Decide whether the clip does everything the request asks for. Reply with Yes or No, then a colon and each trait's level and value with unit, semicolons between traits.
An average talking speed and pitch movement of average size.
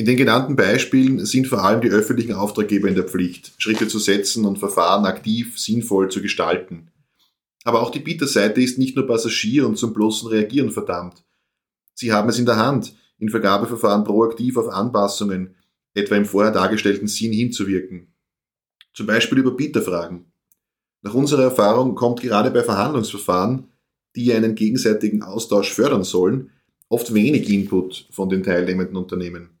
Yes: average, 155 wpm; average, 3.2 semitones